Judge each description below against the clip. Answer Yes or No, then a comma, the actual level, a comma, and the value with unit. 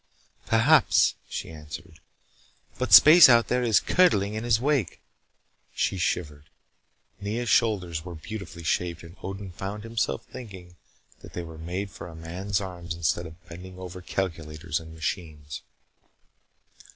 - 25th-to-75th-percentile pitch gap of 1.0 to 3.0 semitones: No, average, 4.4 semitones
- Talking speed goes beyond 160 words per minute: No, average, 140 wpm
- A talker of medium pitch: No, very low, 90 Hz